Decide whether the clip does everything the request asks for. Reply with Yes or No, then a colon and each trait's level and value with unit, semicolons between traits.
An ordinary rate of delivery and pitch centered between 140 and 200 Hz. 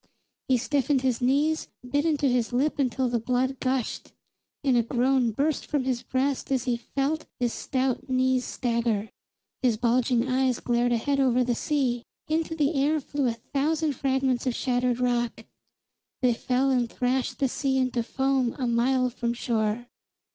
No: average, 165 wpm; very high, 255 Hz